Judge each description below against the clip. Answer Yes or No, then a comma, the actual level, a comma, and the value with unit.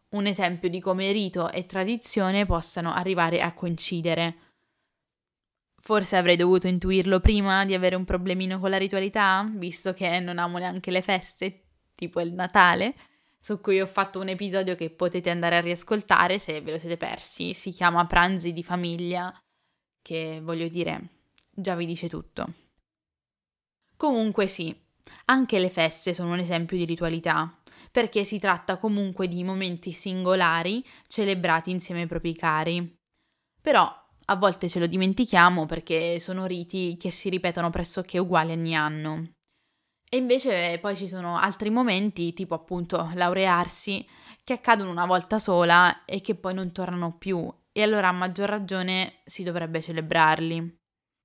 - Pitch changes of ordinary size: No, narrow, 2.0 semitones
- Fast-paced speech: No, average, 150 wpm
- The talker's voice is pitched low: No, medium, 180 Hz